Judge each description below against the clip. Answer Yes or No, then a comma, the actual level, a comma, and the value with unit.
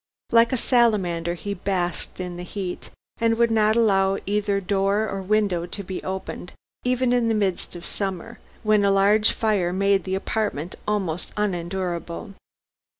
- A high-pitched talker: Yes, high, 195 Hz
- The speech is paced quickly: No, average, 155 wpm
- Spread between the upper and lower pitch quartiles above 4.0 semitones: No, average, 3.0 semitones